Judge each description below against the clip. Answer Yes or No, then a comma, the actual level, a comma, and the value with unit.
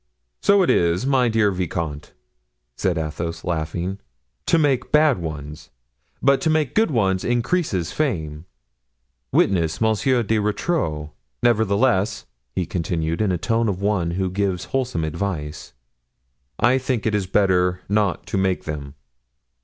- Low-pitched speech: Yes, very low, 95 Hz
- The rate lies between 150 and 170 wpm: No, slow, 135 wpm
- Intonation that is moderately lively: No, wide, 6.2 semitones